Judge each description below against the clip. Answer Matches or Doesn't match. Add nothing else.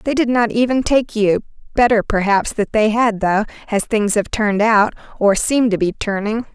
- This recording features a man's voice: Doesn't match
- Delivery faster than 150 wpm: Matches